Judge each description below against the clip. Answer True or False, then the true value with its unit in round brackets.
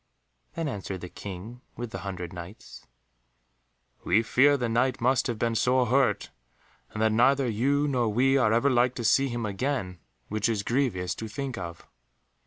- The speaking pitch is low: True (120 Hz)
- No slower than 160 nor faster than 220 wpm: True (175 wpm)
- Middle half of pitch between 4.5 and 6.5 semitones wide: False (4.1 semitones)